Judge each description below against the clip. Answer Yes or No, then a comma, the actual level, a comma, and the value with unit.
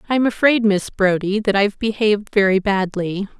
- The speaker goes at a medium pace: Yes, average, 160 wpm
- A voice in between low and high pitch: No, high, 205 Hz